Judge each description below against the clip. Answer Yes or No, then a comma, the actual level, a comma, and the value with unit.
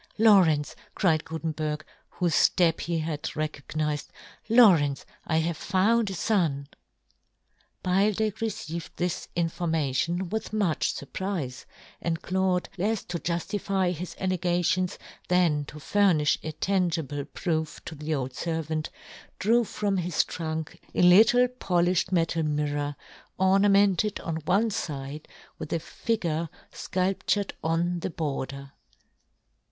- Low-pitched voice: No, medium, 170 Hz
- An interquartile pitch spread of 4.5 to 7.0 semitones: No, average, 3.6 semitones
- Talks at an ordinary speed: No, slow, 125 wpm